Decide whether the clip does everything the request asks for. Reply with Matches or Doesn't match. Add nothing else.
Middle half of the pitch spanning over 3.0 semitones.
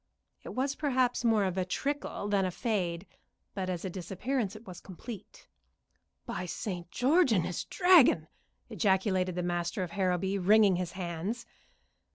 Matches